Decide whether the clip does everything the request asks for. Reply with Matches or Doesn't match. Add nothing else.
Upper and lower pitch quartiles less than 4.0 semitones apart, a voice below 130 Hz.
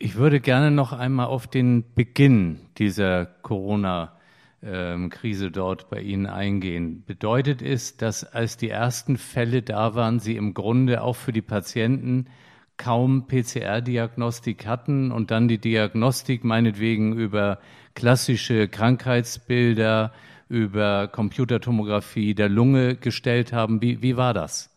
Matches